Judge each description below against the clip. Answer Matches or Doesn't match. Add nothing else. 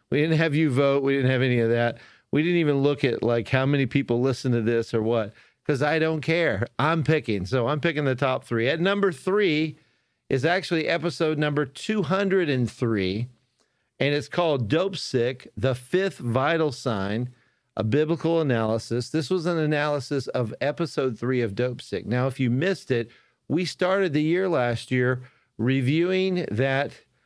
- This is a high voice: Doesn't match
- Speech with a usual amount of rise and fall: Matches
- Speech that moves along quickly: Doesn't match